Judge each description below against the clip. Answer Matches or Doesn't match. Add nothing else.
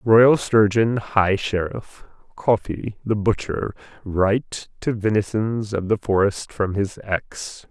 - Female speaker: Doesn't match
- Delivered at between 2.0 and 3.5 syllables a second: Matches